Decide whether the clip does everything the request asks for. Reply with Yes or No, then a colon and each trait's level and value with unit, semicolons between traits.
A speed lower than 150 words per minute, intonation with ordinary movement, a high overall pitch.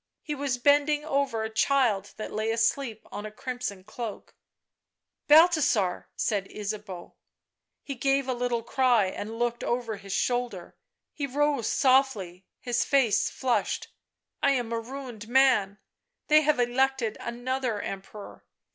Yes: average, 140 wpm; average, 4.1 semitones; high, 240 Hz